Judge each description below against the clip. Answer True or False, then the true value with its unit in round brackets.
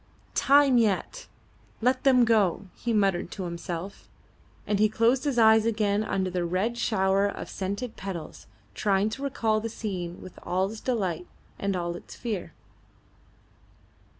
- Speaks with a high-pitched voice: True (205 Hz)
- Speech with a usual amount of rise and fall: True (3.5 semitones)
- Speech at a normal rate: True (150 wpm)